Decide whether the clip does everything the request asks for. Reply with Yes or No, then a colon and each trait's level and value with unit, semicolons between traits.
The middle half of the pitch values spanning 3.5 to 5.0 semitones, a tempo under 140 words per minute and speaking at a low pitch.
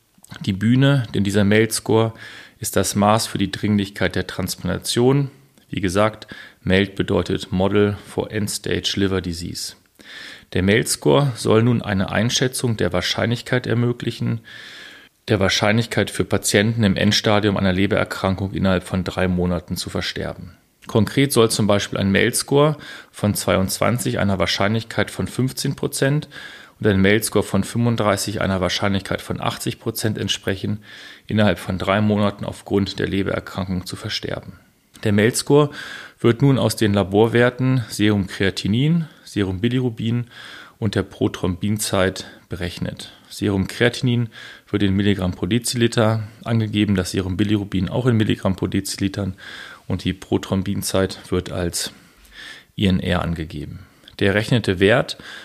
No: average, 3.1 semitones; slow, 125 wpm; low, 105 Hz